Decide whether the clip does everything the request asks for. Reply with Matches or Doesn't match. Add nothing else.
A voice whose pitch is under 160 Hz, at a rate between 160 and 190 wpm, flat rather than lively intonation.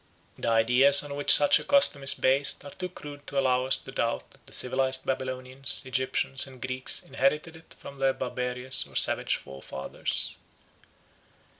Matches